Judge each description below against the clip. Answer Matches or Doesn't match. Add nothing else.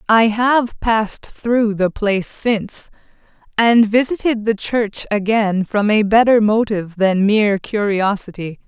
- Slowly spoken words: Matches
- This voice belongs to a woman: Matches